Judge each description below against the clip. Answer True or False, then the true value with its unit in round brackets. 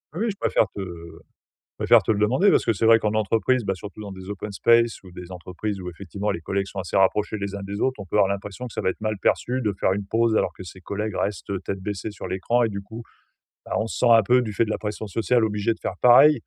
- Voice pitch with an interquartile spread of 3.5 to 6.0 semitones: False (2.7 semitones)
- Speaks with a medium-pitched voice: False (105 Hz)